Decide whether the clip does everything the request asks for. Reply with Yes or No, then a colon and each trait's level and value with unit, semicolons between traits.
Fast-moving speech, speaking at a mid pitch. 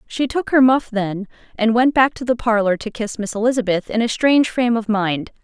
No: fast, 230 wpm; high, 230 Hz